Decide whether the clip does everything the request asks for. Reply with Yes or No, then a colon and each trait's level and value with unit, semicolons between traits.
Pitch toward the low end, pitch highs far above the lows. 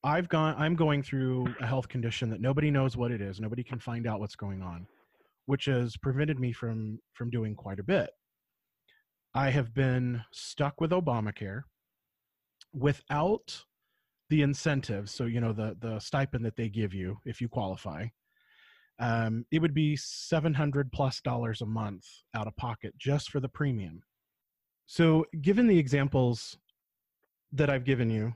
No: low, 125 Hz; average, 4.3 semitones